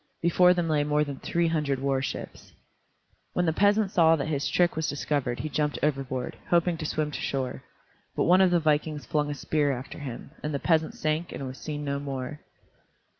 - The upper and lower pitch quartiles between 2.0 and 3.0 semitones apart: Yes, average, 2.7 semitones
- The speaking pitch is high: No, medium, 150 Hz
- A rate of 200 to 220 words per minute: Yes, fast, 205 wpm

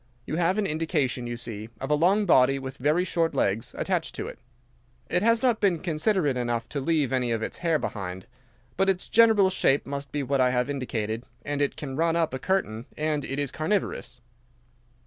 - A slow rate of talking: No, fast, 205 wpm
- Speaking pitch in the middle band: Yes, medium, 145 Hz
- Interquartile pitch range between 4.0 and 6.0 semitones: Yes, average, 5.3 semitones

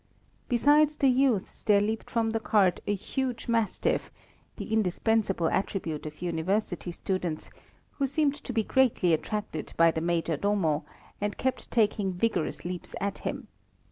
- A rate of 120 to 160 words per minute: Yes, average, 145 wpm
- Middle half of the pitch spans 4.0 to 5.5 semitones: Yes, average, 4.6 semitones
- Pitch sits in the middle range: No, high, 205 Hz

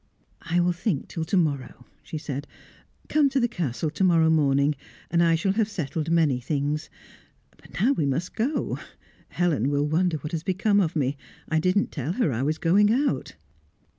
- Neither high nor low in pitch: Yes, medium, 165 Hz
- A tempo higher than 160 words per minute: Yes, average, 185 wpm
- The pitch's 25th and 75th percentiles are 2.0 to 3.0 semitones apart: No, average, 4.2 semitones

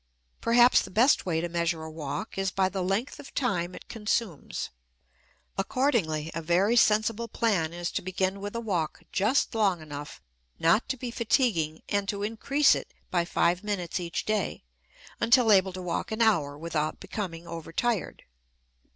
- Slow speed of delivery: No, average, 165 wpm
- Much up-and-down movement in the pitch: No, average, 5.0 semitones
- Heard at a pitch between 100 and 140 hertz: No, high, 190 Hz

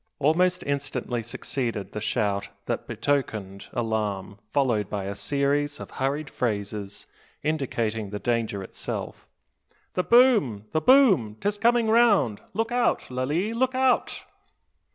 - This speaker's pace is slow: Yes, slow, 125 wpm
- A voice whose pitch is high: No, low, 135 Hz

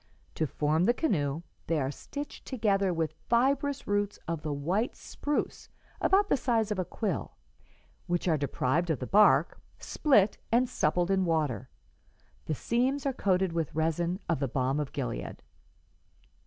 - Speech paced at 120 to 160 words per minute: Yes, average, 155 wpm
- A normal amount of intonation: No, wide, 6.9 semitones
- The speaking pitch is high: No, medium, 175 Hz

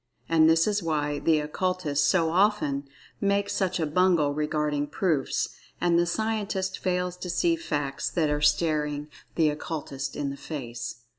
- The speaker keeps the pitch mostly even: No, average, 3.8 semitones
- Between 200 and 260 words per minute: No, average, 155 wpm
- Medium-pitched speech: Yes, medium, 160 Hz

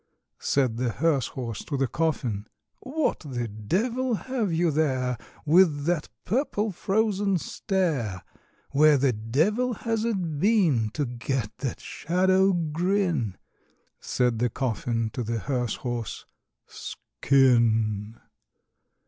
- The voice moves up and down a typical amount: No, wide, 8.0 semitones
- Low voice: No, medium, 145 Hz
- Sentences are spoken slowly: Yes, slow, 115 wpm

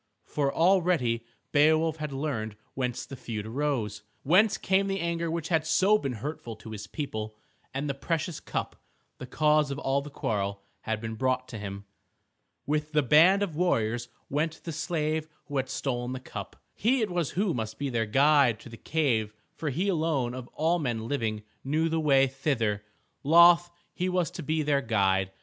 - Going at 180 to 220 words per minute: Yes, average, 185 wpm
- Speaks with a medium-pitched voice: Yes, medium, 145 Hz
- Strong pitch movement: Yes, wide, 5.7 semitones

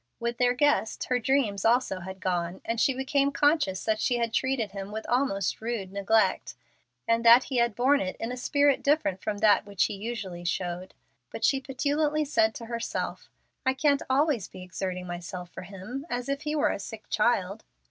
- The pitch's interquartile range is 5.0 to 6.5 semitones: Yes, wide, 5.4 semitones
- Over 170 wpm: Yes, average, 195 wpm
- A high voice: Yes, high, 230 Hz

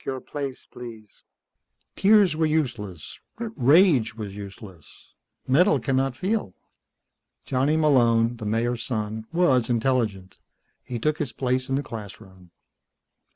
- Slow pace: Yes, slow, 130 wpm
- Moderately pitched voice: No, low, 125 Hz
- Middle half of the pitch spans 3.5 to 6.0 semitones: Yes, average, 5.0 semitones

